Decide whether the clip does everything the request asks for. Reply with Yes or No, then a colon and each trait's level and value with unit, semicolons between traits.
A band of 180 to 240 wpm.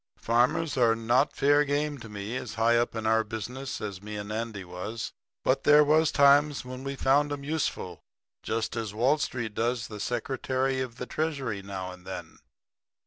Yes: average, 185 wpm